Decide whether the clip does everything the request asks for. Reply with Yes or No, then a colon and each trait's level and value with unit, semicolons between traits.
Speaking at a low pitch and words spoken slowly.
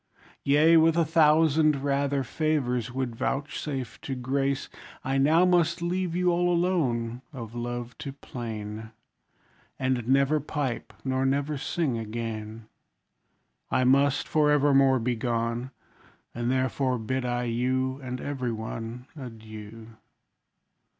Yes: low, 130 Hz; slow, 125 wpm